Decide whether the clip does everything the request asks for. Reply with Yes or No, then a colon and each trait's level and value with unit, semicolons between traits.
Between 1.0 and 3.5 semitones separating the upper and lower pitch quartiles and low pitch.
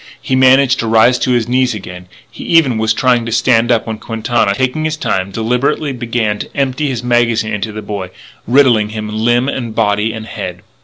Yes: average, 2.8 semitones; low, 115 Hz